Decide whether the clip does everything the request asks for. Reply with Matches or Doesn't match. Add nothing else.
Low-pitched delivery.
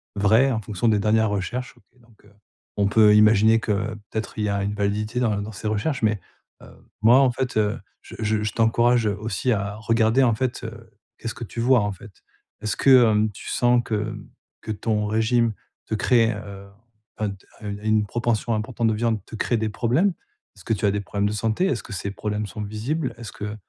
Matches